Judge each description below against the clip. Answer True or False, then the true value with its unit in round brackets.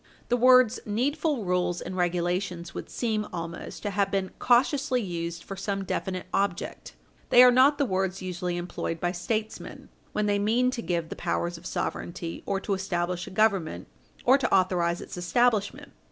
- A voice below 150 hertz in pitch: False (195 Hz)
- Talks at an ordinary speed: True (170 wpm)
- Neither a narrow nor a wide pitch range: True (4.5 semitones)